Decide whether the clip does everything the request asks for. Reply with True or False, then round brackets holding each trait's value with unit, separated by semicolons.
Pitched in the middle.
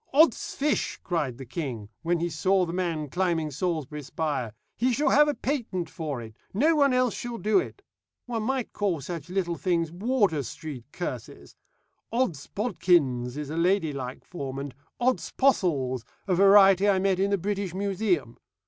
True (180 Hz)